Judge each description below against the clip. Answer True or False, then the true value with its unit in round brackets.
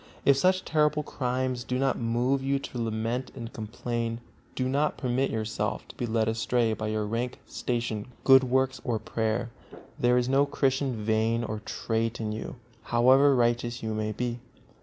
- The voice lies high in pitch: False (120 Hz)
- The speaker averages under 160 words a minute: False (170 wpm)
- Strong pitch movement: False (2.7 semitones)